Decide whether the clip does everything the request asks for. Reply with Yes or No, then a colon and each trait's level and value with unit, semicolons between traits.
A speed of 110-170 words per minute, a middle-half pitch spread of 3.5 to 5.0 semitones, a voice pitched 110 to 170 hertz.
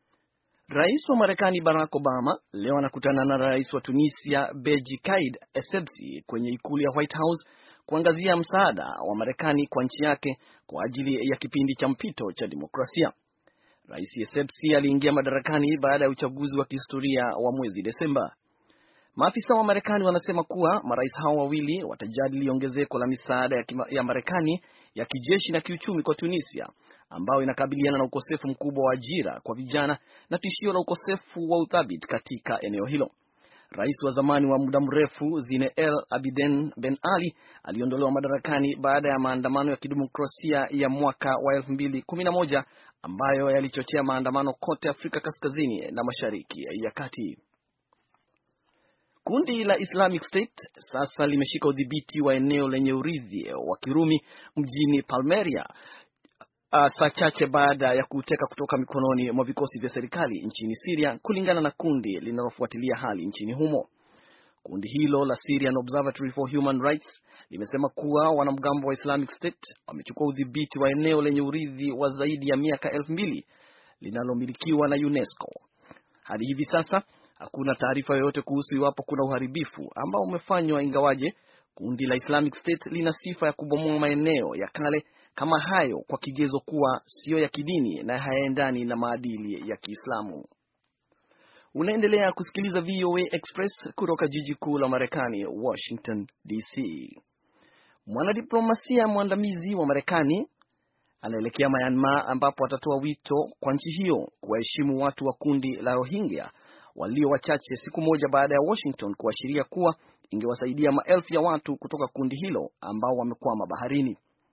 No: average, 135 wpm; average, 2.8 semitones; medium, 140 Hz